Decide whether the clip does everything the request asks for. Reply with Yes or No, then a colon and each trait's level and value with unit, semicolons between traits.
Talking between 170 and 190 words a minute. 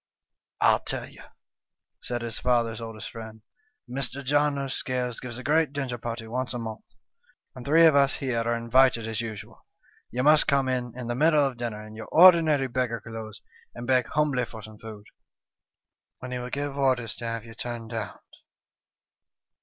Yes: average, 185 wpm